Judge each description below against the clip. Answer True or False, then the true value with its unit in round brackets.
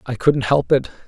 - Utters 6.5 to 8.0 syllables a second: False (4.9 syllables/s)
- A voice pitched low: True (120 Hz)